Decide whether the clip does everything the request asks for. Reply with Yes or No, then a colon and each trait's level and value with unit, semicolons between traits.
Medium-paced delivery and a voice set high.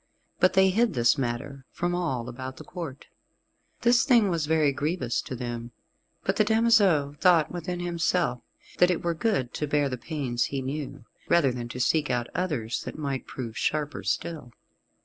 No: average, 175 wpm; medium, 150 Hz